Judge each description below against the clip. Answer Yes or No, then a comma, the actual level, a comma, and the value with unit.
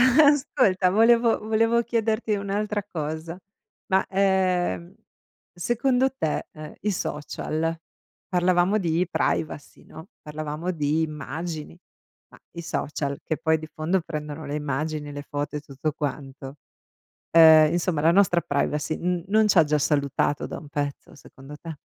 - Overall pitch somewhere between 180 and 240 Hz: No, medium, 160 Hz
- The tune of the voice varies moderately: Yes, average, 4.4 semitones